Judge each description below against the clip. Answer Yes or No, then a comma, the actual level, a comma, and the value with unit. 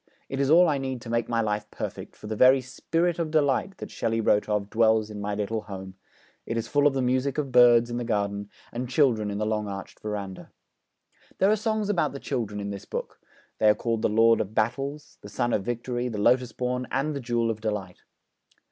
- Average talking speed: No, fast, 230 wpm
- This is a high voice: No, low, 115 Hz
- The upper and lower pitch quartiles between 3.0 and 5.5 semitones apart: Yes, average, 4.2 semitones